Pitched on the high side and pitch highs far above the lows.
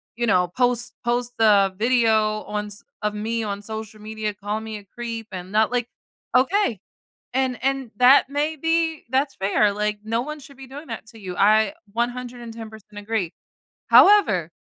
No: high, 225 Hz; average, 3.1 semitones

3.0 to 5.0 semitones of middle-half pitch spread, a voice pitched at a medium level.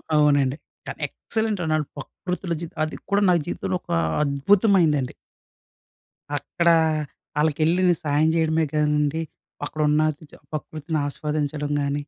No: narrow, 2.5 semitones; medium, 155 Hz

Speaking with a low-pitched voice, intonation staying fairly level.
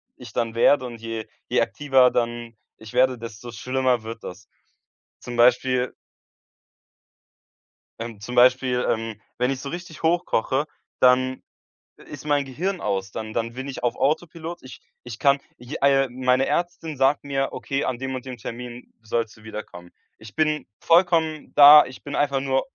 No: low, 130 Hz; average, 3.1 semitones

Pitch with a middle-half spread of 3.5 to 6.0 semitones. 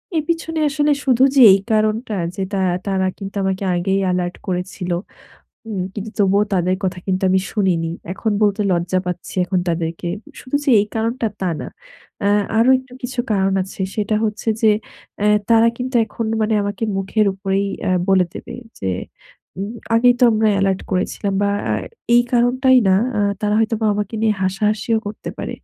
No: average, 3.1 semitones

